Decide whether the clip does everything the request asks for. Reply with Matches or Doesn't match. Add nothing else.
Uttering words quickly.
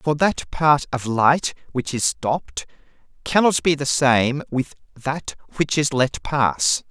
Doesn't match